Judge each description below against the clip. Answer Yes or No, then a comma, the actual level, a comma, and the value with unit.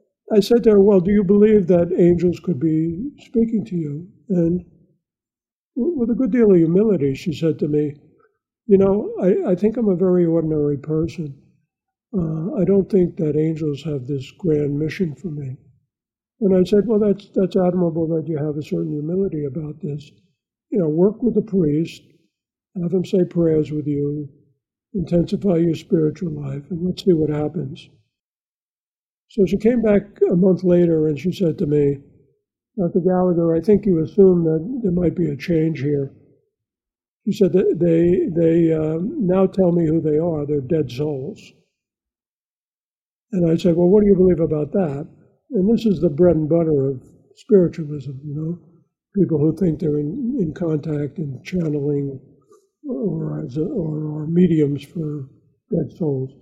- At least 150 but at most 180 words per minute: Yes, average, 175 wpm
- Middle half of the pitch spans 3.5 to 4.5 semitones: Yes, average, 4.0 semitones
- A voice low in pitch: No, medium, 170 Hz